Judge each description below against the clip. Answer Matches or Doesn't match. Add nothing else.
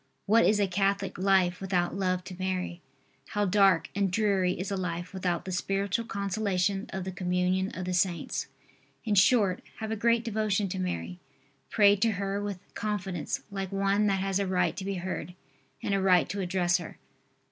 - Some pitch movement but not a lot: Doesn't match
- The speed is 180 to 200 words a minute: Matches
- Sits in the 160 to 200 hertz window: Matches